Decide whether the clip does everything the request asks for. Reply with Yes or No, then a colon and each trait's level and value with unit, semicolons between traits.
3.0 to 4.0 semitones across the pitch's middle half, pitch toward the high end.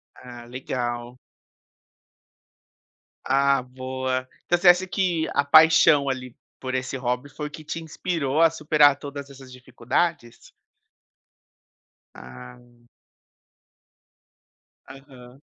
No: average, 3.3 semitones; low, 135 Hz